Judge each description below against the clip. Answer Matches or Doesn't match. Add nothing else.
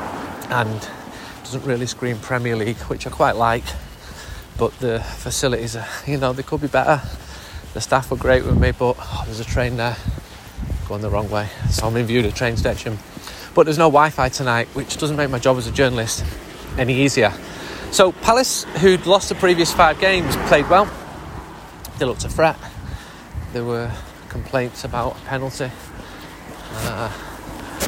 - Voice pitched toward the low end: Matches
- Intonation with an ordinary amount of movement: Matches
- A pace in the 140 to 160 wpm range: Doesn't match